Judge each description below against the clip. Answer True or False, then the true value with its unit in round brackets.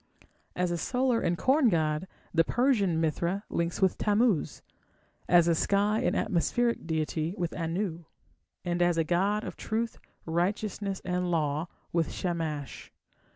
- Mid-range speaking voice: True (175 Hz)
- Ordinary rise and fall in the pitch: True (3.8 semitones)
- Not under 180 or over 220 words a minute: False (140 wpm)